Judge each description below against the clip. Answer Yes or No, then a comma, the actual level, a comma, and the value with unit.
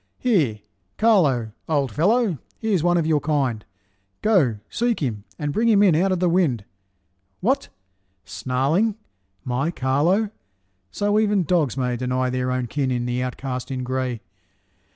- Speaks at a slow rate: No, average, 150 wpm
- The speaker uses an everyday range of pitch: No, wide, 7.0 semitones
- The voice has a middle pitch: Yes, medium, 145 Hz